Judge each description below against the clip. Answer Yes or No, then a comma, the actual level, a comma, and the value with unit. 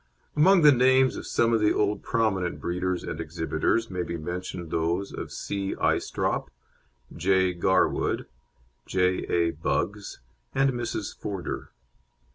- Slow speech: Yes, slow, 120 wpm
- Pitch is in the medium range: No, very low, 95 Hz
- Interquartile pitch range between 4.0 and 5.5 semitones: Yes, average, 4.7 semitones